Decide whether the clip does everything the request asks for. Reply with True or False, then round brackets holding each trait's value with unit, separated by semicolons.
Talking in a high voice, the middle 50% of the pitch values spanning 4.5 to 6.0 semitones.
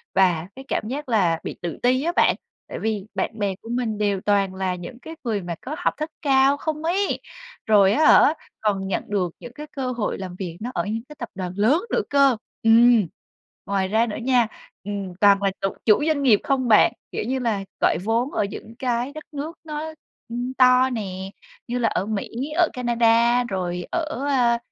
True (230 Hz; 4.9 semitones)